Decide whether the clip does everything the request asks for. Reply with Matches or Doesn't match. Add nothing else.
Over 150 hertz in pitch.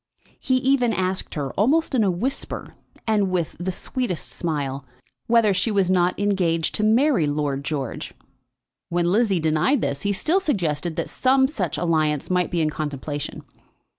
Matches